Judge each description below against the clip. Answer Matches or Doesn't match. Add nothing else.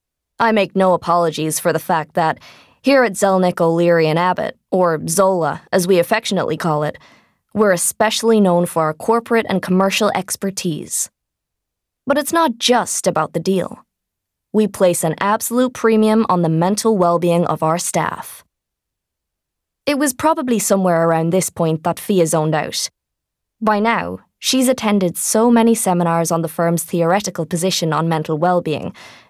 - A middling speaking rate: Matches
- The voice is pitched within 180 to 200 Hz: Matches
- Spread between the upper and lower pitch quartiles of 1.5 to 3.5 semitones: Doesn't match